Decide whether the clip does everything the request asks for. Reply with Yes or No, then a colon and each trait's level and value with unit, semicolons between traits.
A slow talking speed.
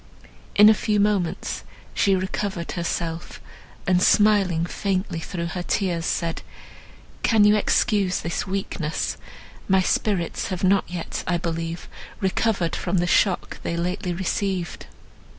Yes: slow, 130 wpm